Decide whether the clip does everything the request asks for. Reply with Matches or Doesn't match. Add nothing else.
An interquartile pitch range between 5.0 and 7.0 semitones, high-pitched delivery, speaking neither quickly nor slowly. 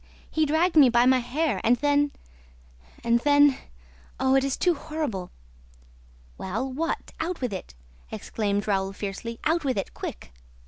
Matches